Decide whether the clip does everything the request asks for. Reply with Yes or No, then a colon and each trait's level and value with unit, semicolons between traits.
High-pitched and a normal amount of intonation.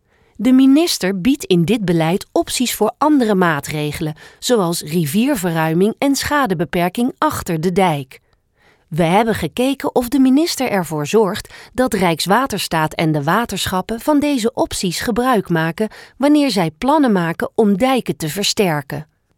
No: high, 200 Hz; wide, 7.1 semitones